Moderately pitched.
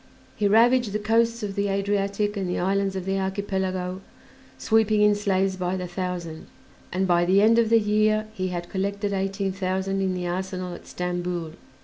No: high, 195 Hz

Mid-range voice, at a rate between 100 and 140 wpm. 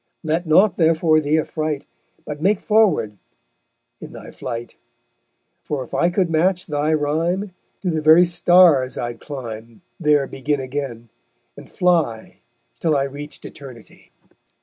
Yes: medium, 155 Hz; slow, 135 wpm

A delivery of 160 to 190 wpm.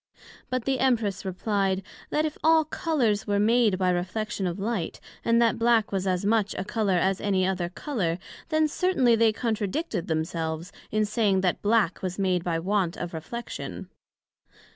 Yes: average, 165 wpm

